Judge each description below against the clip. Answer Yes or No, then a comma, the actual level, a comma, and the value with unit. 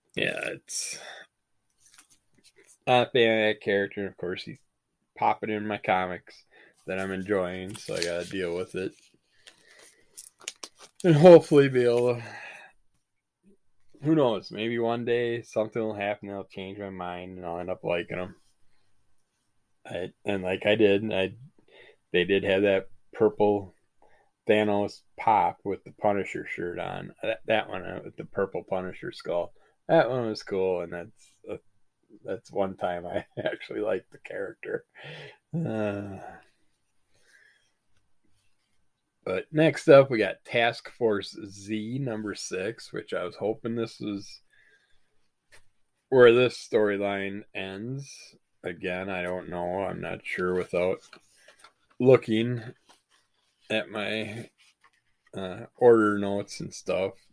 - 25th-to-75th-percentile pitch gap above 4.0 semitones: No, average, 3.7 semitones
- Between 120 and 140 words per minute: Yes, slow, 135 wpm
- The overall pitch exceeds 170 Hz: No, low, 105 Hz